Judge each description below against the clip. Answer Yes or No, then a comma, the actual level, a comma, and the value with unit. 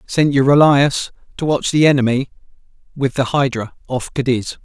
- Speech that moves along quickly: No, average, 140 wpm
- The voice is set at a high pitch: No, low, 135 Hz